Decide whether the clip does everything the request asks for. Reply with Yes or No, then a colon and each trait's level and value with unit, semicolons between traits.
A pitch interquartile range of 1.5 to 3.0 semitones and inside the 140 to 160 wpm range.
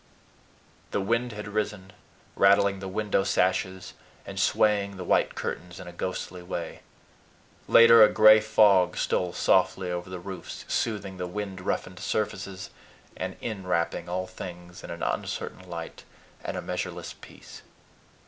Yes: narrow, 2.5 semitones; average, 145 wpm